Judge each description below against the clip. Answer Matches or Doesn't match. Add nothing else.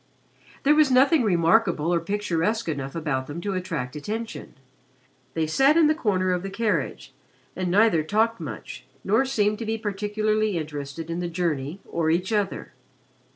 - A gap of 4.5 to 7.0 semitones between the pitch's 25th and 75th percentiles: Matches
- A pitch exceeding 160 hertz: Matches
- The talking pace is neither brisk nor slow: Matches